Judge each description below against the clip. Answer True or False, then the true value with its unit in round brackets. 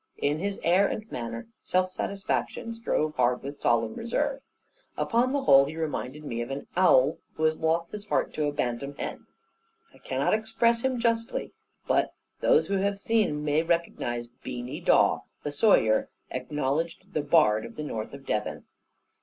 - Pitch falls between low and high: True (155 Hz)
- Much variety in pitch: True (7.4 semitones)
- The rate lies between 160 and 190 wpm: True (170 wpm)